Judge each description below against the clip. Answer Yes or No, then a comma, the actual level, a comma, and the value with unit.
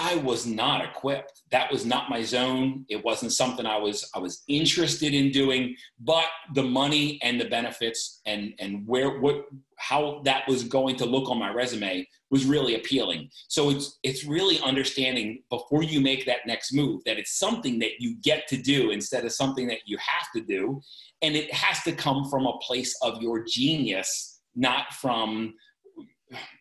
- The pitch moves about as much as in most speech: Yes, average, 3.3 semitones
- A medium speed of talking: Yes, average, 185 wpm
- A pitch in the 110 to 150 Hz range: Yes, low, 135 Hz